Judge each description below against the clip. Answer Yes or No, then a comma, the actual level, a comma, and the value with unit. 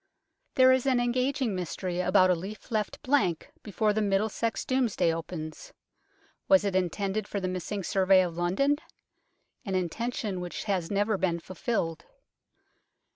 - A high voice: Yes, high, 200 Hz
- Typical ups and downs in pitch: Yes, average, 4.2 semitones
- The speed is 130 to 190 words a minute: Yes, average, 140 wpm